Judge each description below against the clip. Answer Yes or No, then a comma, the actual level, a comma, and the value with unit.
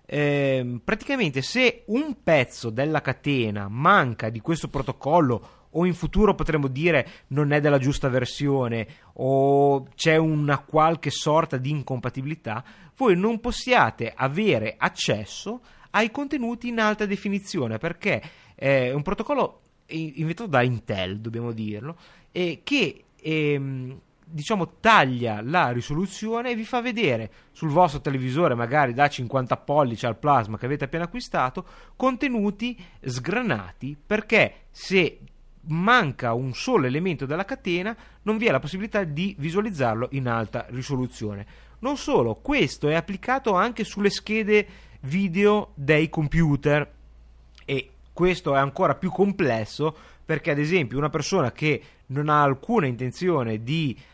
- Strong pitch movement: Yes, wide, 6.8 semitones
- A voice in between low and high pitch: Yes, medium, 150 Hz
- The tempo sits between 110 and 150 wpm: Yes, average, 135 wpm